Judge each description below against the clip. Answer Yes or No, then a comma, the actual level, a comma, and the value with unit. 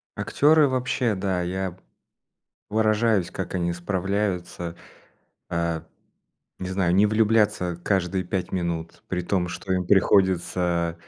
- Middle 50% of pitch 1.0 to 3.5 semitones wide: Yes, average, 2.8 semitones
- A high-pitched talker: No, very low, 95 Hz